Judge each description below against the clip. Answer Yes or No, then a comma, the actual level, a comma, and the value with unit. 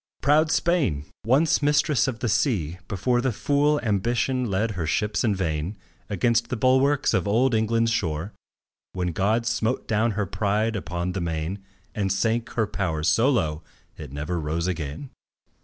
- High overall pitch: No, low, 105 Hz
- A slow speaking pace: No, average, 160 wpm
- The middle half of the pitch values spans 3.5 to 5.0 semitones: No, wide, 5.4 semitones